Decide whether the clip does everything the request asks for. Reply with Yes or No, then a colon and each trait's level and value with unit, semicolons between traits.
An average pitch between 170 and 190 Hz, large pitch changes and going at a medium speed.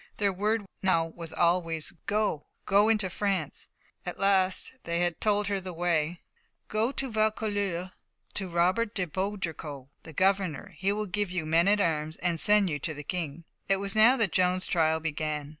No: medium, 185 Hz; average, 3.8 semitones; average, 175 wpm